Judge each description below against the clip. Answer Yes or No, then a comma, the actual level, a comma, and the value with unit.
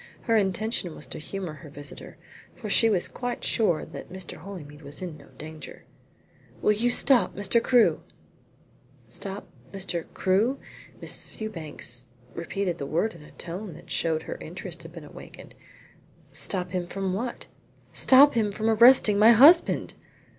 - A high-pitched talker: Yes, high, 195 Hz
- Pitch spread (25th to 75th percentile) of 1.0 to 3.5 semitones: No, average, 5.1 semitones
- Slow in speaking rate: No, average, 155 wpm